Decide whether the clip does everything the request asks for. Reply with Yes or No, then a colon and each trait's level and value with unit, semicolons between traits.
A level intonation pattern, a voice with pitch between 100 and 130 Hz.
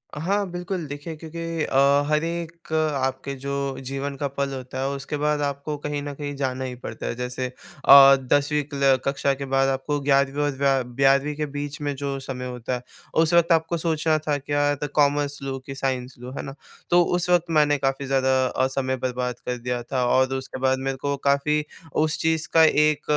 No: narrow, 2.3 semitones; medium, 140 Hz